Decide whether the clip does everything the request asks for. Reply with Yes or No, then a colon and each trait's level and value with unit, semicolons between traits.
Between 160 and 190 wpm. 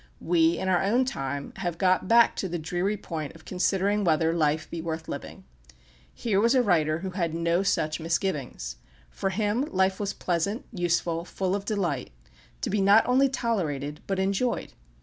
Yes: average, 175 wpm